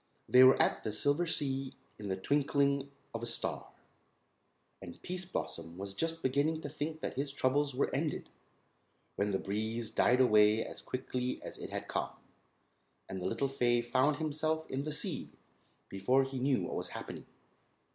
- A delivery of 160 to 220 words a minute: Yes, average, 170 wpm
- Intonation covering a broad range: No, average, 4.3 semitones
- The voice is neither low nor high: No, low, 130 Hz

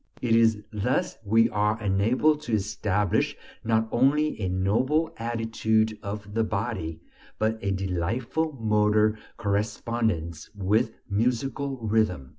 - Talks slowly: Yes, slow, 115 wpm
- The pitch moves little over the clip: Yes, narrow, 2.3 semitones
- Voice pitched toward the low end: Yes, low, 110 Hz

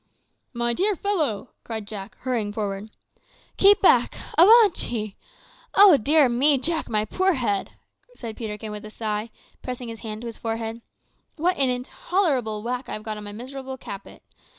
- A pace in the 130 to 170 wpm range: Yes, average, 165 wpm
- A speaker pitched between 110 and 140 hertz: No, high, 235 Hz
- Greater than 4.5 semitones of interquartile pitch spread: Yes, average, 5.2 semitones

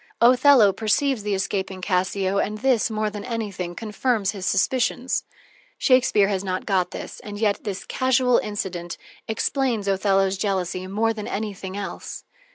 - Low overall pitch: No, high, 205 Hz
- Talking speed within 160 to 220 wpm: No, average, 145 wpm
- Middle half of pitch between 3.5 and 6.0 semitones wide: No, average, 2.9 semitones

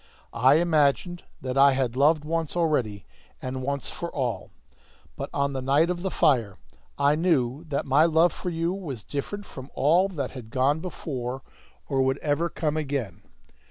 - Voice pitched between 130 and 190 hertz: Yes, medium, 140 Hz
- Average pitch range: Yes, average, 3.9 semitones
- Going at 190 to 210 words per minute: No, average, 170 wpm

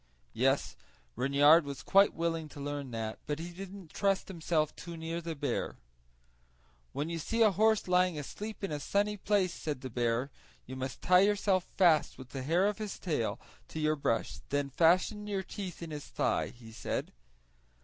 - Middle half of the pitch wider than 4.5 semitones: Yes, average, 5.2 semitones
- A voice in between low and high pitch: Yes, medium, 165 Hz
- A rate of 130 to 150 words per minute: No, average, 185 wpm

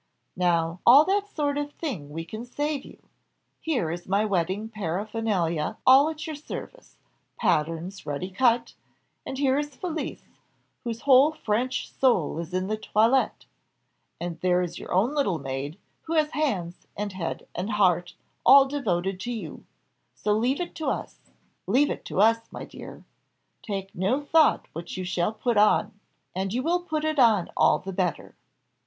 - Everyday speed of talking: Yes, average, 165 wpm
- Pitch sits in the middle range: No, high, 215 Hz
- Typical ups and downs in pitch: No, wide, 7.5 semitones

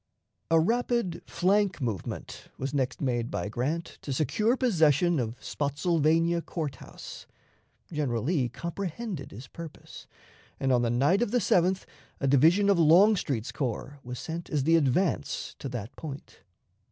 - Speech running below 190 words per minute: Yes, average, 145 wpm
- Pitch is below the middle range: No, medium, 155 Hz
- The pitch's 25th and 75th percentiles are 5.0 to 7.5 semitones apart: Yes, wide, 5.4 semitones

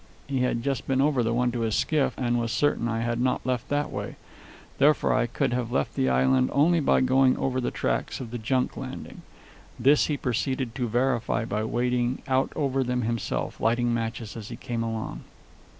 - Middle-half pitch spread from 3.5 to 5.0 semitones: No, narrow, 2.4 semitones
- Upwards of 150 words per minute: Yes, average, 200 wpm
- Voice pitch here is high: No, low, 120 Hz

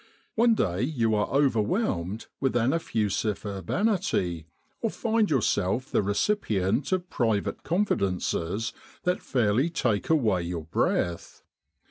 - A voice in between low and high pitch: No, low, 115 Hz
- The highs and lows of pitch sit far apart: Yes, wide, 9.0 semitones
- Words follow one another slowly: Yes, slow, 120 wpm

